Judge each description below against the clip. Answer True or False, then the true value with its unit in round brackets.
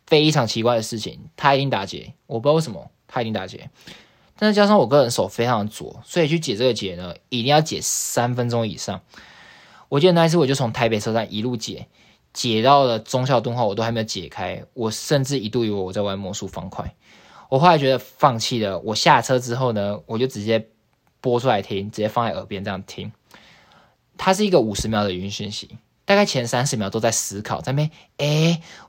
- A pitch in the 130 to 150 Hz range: False (120 Hz)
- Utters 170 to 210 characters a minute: False (315 characters per minute)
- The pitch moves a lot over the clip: False (4.8 semitones)